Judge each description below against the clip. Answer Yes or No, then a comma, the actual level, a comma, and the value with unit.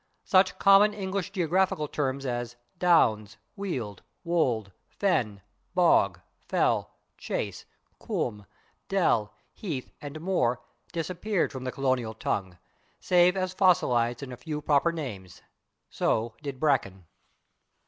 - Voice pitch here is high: No, medium, 140 Hz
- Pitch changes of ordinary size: No, wide, 7.3 semitones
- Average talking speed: No, slow, 115 wpm